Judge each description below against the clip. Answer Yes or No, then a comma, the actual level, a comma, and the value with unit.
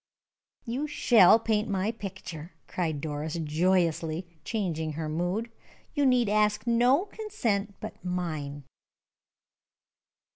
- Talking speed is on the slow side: Yes, slow, 105 wpm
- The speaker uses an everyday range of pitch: No, wide, 6.3 semitones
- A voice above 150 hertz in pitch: Yes, high, 190 Hz